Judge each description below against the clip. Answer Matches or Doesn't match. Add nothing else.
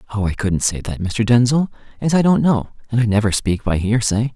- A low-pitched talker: Matches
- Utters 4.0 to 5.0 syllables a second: Doesn't match